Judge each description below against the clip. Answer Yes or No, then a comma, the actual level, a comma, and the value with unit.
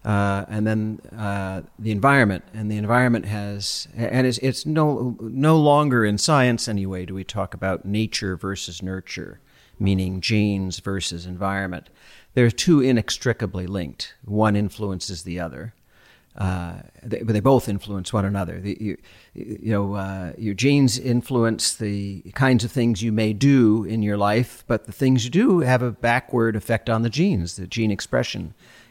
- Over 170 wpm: No, average, 165 wpm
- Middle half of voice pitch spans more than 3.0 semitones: Yes, average, 3.7 semitones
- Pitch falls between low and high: No, low, 105 Hz